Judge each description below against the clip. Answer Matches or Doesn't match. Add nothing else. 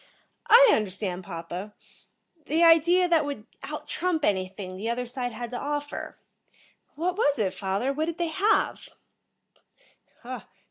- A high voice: Matches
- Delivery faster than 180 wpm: Doesn't match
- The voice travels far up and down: Matches